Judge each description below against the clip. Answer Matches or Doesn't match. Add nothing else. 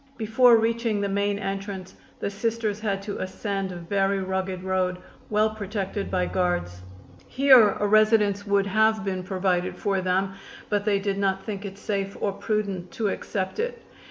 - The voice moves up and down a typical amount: Doesn't match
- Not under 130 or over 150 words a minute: Doesn't match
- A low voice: Doesn't match